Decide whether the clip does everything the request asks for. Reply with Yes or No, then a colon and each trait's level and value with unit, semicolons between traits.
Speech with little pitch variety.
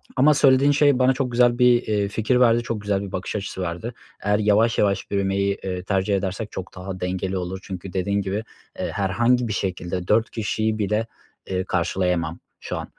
No: average, 3.7 semitones